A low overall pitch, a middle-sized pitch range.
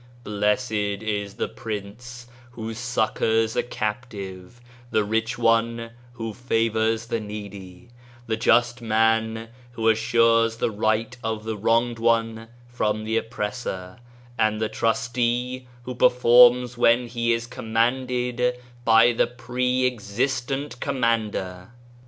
No: low, 115 Hz; narrow, 1.9 semitones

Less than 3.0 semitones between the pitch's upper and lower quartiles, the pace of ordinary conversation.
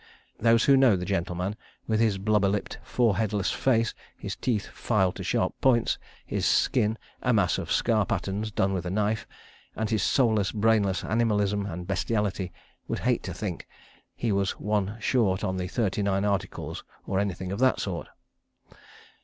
Yes: narrow, 2.5 semitones; average, 165 wpm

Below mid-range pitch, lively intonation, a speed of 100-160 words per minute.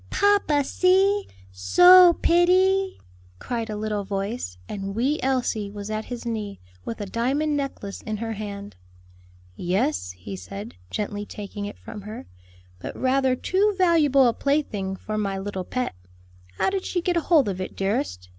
No: high, 225 Hz; wide, 7.2 semitones; average, 155 wpm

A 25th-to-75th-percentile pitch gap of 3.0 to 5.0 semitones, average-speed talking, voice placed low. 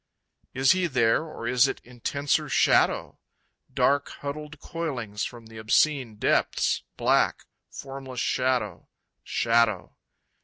No: average, 3.7 semitones; slow, 110 wpm; low, 130 Hz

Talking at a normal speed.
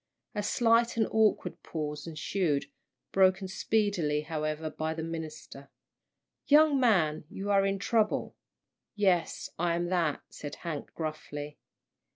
No: slow, 125 wpm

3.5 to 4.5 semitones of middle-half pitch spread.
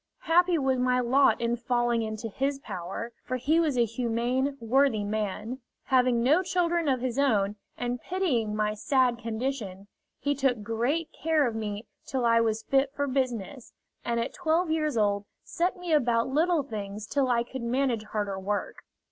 Yes: average, 4.0 semitones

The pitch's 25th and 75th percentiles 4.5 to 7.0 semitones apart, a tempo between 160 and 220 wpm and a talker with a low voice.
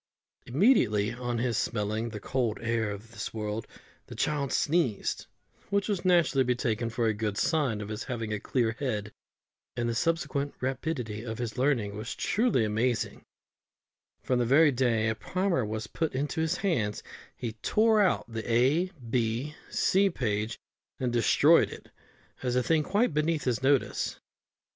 Yes: average, 5.2 semitones; average, 165 wpm; low, 120 Hz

